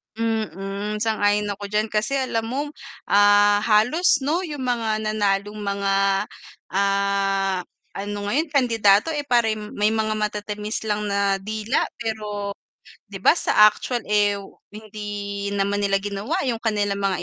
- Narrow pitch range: Yes, narrow, 1.7 semitones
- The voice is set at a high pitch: Yes, high, 210 Hz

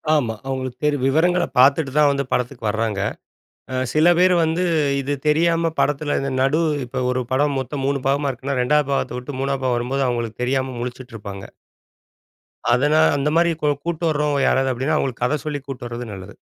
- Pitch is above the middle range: No, low, 135 Hz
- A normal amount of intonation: Yes, average, 3.0 semitones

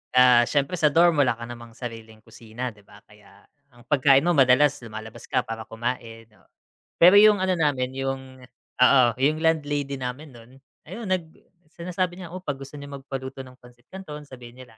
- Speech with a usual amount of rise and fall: Yes, average, 4.0 semitones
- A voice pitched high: No, low, 135 Hz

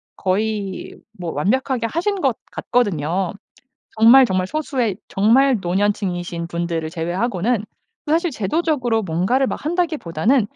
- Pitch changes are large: Yes, wide, 6.7 semitones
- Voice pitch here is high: Yes, high, 215 Hz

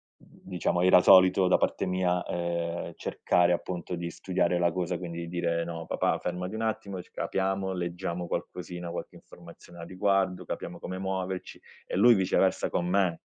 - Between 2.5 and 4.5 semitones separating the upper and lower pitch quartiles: No, narrow, 1.5 semitones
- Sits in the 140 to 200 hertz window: No, very low, 90 Hz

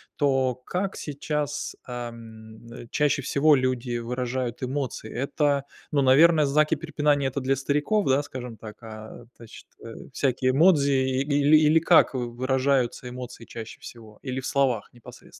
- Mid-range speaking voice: No, low, 130 Hz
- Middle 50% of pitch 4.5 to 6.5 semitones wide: No, average, 3.1 semitones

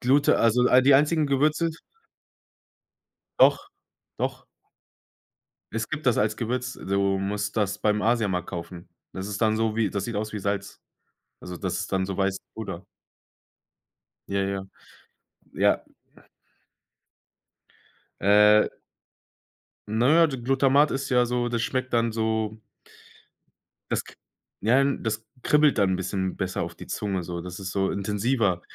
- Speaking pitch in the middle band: No, low, 110 Hz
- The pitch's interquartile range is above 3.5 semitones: Yes, average, 4.3 semitones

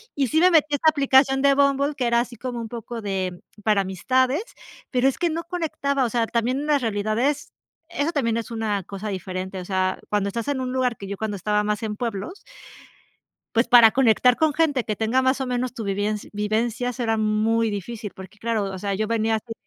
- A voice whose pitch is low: No, high, 230 Hz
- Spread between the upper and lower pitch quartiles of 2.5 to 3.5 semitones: No, average, 4.1 semitones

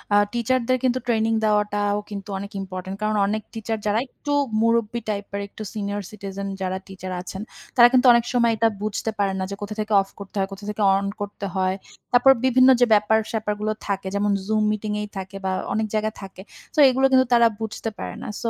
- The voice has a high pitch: Yes, high, 215 Hz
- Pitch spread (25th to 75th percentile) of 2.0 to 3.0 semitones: Yes, narrow, 2.5 semitones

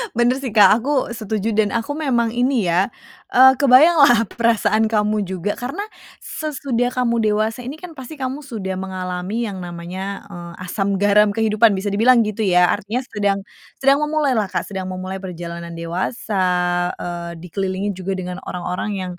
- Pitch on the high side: Yes, high, 210 Hz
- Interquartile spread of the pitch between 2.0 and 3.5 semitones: No, average, 4.6 semitones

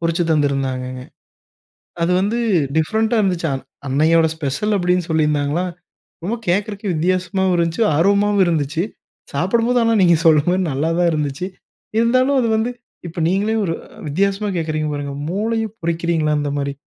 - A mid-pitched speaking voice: Yes, medium, 170 Hz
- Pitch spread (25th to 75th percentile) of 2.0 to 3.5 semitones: No, average, 4.7 semitones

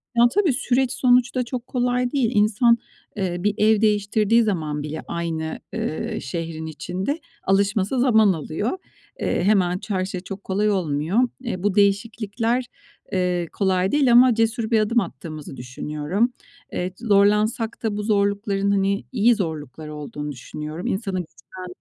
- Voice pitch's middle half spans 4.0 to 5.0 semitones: Yes, average, 4.6 semitones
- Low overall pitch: No, high, 200 Hz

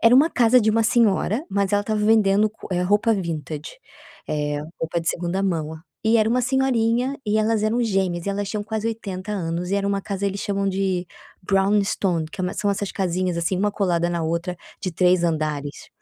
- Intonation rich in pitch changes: No, average, 3.8 semitones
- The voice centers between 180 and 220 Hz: Yes, high, 195 Hz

